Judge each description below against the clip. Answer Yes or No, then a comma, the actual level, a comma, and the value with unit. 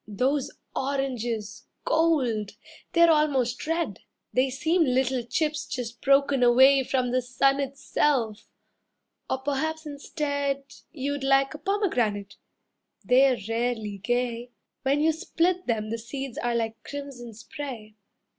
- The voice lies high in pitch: Yes, very high, 265 Hz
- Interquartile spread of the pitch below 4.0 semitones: Yes, average, 3.2 semitones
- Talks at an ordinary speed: No, slow, 120 wpm